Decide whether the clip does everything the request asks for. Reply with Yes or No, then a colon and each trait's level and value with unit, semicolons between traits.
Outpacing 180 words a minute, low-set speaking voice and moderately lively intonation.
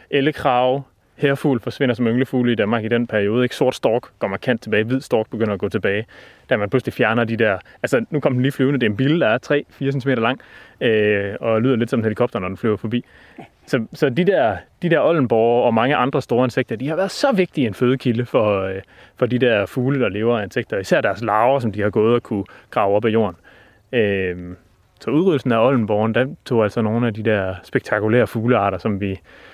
Yes: average, 220 wpm; low, 120 Hz; average, 3.5 semitones